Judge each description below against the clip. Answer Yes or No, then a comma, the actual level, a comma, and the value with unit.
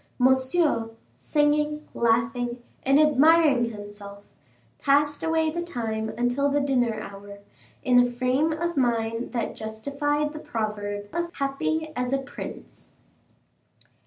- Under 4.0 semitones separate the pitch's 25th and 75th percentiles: No, average, 4.6 semitones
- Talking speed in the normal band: No, slow, 120 wpm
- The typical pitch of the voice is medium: No, very high, 260 Hz